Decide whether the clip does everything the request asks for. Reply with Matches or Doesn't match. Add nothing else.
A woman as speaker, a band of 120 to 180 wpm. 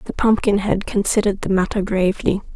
Matches